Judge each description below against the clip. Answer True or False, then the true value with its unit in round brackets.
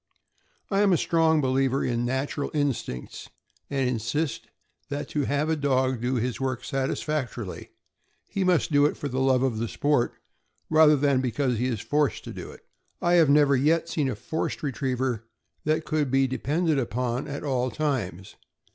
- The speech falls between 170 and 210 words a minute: True (175 wpm)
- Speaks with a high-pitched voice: False (135 Hz)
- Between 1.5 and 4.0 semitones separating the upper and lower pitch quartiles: True (3.0 semitones)